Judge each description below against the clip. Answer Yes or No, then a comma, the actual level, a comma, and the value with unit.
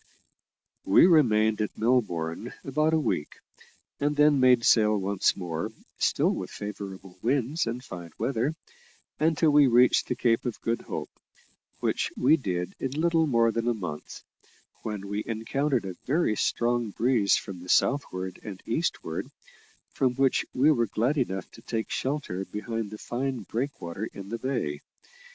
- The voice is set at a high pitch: No, low, 115 Hz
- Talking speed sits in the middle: Yes, average, 155 wpm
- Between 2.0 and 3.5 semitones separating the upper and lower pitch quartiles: No, average, 5.3 semitones